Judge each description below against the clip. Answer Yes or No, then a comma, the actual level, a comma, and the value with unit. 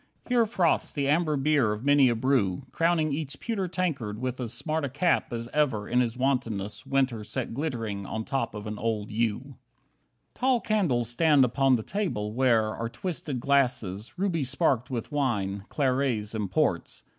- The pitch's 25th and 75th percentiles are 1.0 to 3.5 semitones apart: No, average, 5.1 semitones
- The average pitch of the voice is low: Yes, low, 130 Hz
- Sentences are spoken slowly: No, average, 175 wpm